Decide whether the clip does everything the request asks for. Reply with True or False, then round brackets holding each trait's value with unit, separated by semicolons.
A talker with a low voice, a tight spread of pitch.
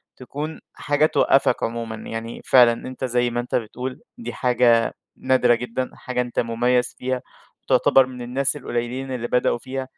True (125 Hz; 1.5 semitones)